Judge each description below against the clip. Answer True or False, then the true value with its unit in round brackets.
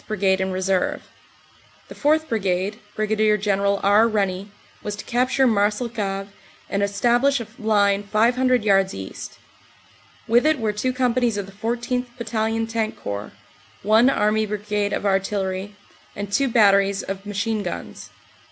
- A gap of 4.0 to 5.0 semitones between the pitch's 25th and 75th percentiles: False (2.7 semitones)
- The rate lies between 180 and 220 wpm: False (145 wpm)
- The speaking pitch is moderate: False (210 Hz)